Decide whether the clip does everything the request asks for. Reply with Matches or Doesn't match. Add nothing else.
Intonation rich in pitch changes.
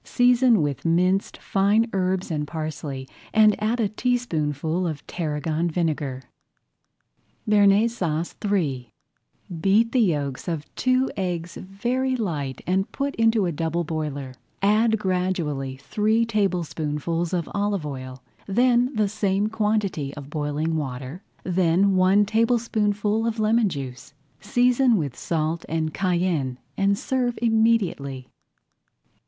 Matches